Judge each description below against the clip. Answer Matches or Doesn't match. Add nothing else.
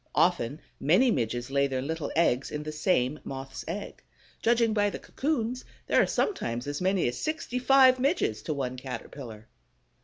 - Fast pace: Doesn't match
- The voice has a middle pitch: Matches